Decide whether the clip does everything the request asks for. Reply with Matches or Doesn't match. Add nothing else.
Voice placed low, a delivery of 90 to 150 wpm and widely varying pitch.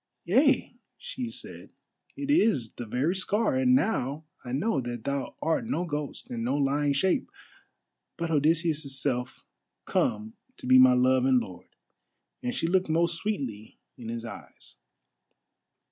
Doesn't match